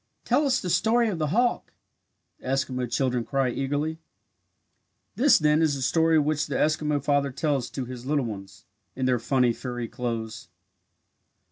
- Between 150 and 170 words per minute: Yes, average, 160 wpm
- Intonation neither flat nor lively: Yes, average, 3.7 semitones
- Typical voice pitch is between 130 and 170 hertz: Yes, medium, 140 Hz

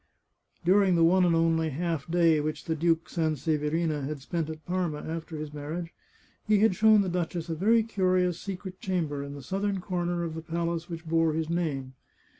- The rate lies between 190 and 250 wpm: Yes, average, 195 wpm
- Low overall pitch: No, medium, 165 Hz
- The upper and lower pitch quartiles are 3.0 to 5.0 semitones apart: No, narrow, 2.4 semitones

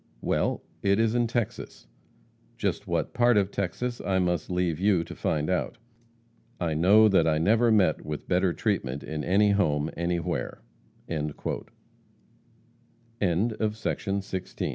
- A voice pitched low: Yes, very low, 95 Hz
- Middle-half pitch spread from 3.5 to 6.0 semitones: Yes, average, 4.8 semitones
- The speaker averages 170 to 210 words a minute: No, average, 145 wpm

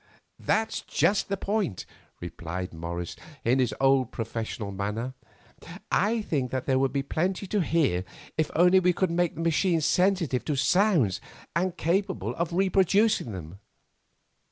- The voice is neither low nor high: Yes, medium, 160 Hz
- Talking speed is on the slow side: No, average, 145 wpm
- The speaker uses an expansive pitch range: Yes, wide, 8.3 semitones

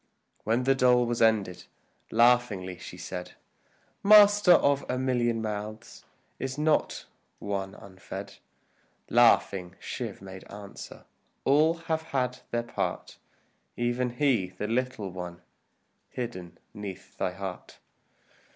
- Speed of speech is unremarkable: No, slow, 115 wpm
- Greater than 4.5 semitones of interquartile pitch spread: Yes, average, 5.0 semitones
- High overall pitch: No, low, 120 Hz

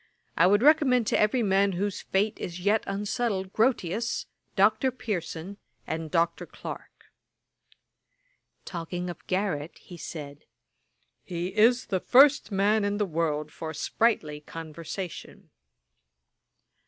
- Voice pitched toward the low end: No, high, 190 Hz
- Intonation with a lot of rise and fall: No, average, 4.4 semitones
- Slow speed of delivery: Yes, slow, 115 wpm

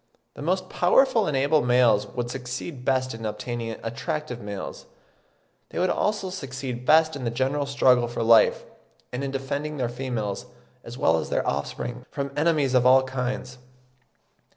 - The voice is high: No, low, 130 Hz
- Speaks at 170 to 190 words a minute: No, average, 160 wpm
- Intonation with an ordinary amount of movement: Yes, average, 3.2 semitones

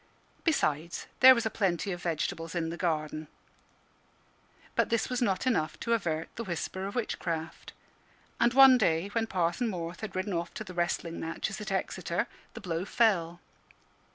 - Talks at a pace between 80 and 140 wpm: No, average, 165 wpm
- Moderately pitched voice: Yes, medium, 180 Hz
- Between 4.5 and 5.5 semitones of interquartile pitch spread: Yes, average, 5.0 semitones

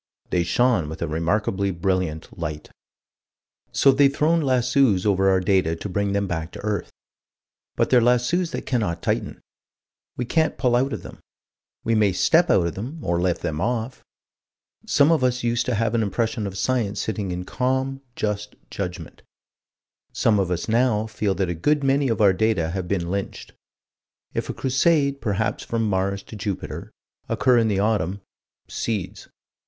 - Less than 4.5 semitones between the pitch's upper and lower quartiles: No, average, 5.0 semitones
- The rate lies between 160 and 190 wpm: Yes, average, 170 wpm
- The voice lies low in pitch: Yes, low, 105 Hz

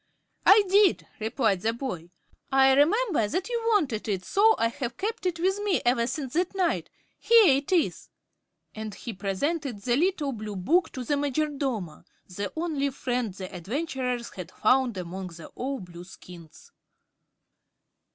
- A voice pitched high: Yes, very high, 265 Hz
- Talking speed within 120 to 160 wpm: Yes, average, 155 wpm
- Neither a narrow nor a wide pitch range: No, wide, 8.1 semitones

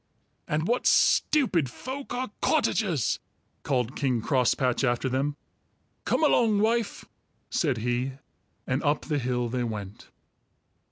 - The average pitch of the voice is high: No, low, 135 Hz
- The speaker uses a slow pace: Yes, slow, 120 wpm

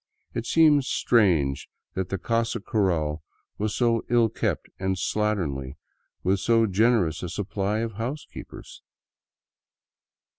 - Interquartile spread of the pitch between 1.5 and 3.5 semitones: No, average, 4.2 semitones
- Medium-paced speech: No, slow, 120 wpm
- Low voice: Yes, low, 105 Hz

